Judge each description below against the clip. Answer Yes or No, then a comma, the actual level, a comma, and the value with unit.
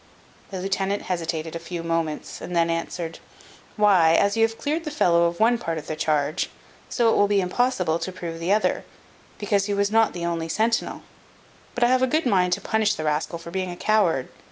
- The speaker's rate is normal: No, fast, 215 wpm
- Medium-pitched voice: Yes, medium, 180 Hz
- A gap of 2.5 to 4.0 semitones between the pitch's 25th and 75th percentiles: No, average, 4.4 semitones